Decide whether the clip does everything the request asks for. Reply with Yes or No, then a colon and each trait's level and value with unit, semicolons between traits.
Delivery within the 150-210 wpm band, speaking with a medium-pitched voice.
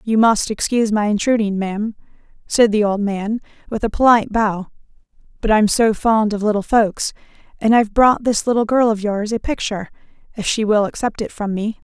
No: average, 190 wpm; high, 215 Hz